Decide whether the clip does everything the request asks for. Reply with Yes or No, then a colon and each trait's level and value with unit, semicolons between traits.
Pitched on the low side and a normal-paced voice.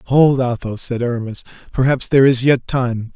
Yes: low, 125 Hz; average, 170 wpm